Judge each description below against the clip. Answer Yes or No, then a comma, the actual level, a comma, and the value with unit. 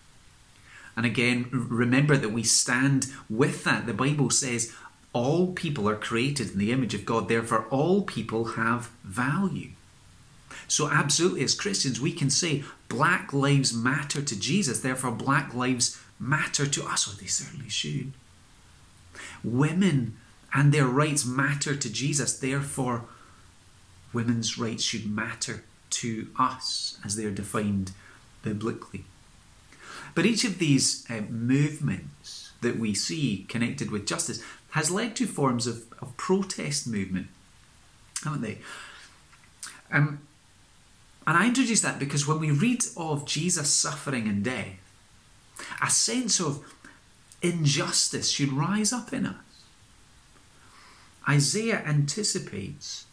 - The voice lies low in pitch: Yes, low, 130 Hz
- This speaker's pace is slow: Yes, slow, 130 wpm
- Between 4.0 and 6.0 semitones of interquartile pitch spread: Yes, average, 4.7 semitones